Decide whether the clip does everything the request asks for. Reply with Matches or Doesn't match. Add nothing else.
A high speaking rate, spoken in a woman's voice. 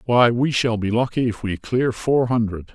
Doesn't match